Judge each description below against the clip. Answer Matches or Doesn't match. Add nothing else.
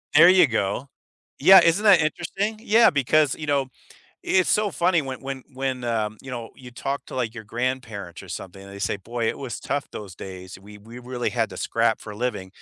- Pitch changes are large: Matches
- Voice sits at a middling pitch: Doesn't match